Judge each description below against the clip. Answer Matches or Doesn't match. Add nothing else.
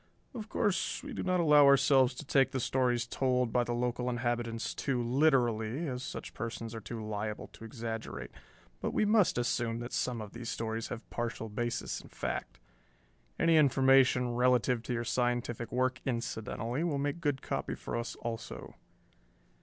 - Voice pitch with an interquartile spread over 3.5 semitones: Doesn't match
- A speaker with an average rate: Matches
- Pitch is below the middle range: Matches